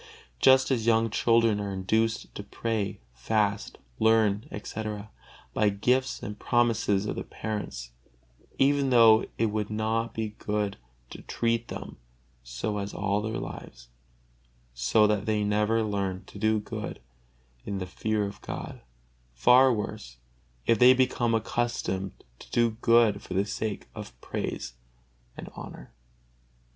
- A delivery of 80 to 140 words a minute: Yes, slow, 135 wpm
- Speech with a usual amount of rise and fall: No, narrow, 2.2 semitones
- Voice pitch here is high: No, low, 110 Hz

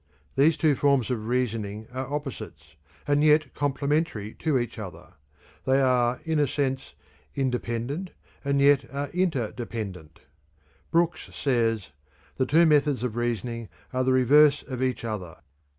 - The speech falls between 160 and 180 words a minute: No, slow, 135 wpm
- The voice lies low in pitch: Yes, low, 130 Hz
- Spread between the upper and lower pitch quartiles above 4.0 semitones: No, average, 3.7 semitones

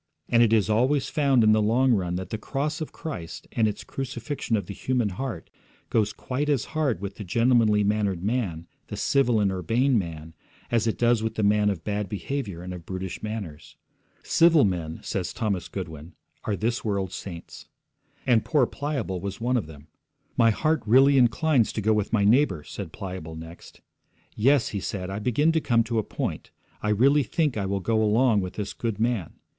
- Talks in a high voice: No, low, 110 Hz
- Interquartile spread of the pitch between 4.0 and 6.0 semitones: Yes, average, 4.6 semitones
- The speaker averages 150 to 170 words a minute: No, average, 195 wpm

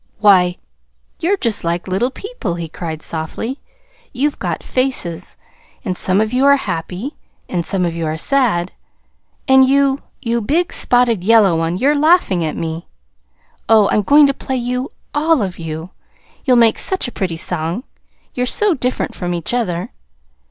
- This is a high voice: Yes, high, 220 Hz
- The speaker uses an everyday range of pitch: No, wide, 7.3 semitones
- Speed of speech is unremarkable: Yes, average, 165 wpm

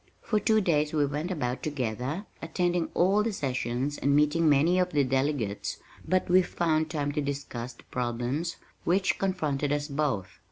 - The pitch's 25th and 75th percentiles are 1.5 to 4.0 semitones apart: No, average, 4.4 semitones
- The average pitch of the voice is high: No, medium, 150 Hz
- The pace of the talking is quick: No, average, 165 wpm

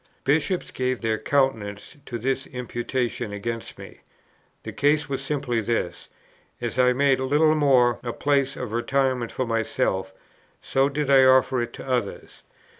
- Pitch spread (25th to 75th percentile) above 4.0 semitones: No, average, 2.7 semitones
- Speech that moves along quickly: No, average, 145 wpm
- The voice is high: No, low, 130 Hz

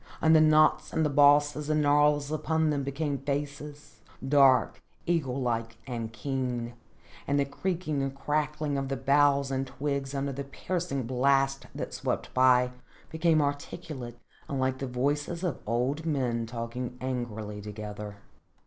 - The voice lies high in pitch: No, medium, 140 Hz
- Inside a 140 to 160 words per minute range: Yes, average, 145 wpm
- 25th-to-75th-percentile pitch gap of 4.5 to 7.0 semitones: No, average, 2.8 semitones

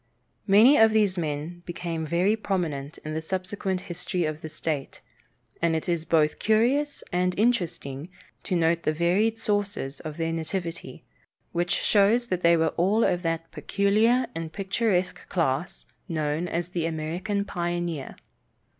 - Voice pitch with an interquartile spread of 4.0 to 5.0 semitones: No, average, 3.6 semitones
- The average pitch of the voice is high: No, medium, 175 Hz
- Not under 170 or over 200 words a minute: No, average, 145 wpm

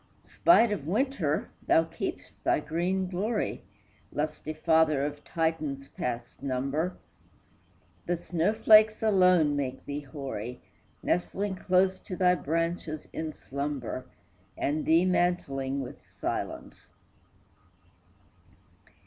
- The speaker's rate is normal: No, slow, 105 wpm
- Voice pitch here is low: No, medium, 160 Hz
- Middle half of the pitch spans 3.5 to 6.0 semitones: Yes, average, 4.4 semitones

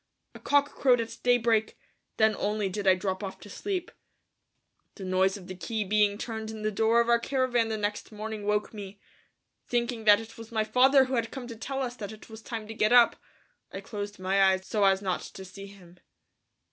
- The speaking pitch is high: Yes, high, 215 Hz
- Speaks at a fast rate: Yes, fast, 215 wpm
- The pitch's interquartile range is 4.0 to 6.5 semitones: No, average, 2.8 semitones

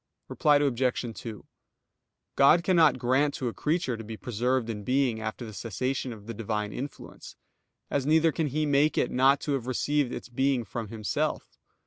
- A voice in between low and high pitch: No, low, 130 Hz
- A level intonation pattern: No, average, 4.0 semitones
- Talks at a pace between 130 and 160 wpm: No, average, 175 wpm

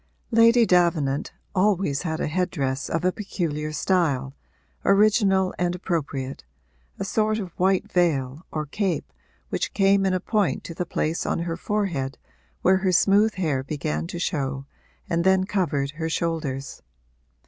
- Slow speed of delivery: No, average, 150 wpm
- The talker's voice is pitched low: No, medium, 175 Hz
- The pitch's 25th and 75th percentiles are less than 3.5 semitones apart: No, average, 4.8 semitones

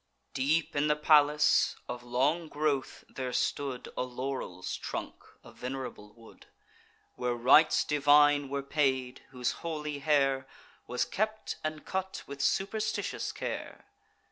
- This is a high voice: No, medium, 140 Hz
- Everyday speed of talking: No, slow, 125 wpm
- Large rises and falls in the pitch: No, average, 2.9 semitones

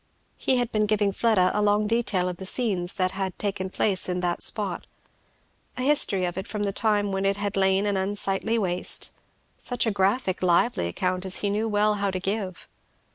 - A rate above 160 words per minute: Yes, average, 200 wpm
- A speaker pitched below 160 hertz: No, high, 200 Hz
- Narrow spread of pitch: Yes, narrow, 2.1 semitones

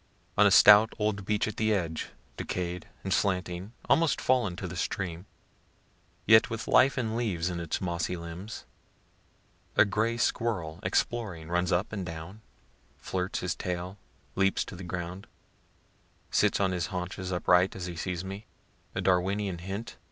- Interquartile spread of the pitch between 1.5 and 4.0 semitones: Yes, average, 3.1 semitones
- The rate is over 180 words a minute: No, average, 155 wpm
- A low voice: Yes, very low, 95 Hz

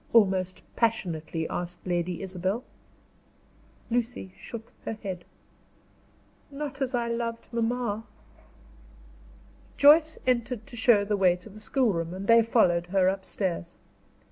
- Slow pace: Yes, slow, 115 wpm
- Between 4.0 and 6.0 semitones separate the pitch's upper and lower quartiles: Yes, average, 4.5 semitones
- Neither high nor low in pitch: No, high, 215 Hz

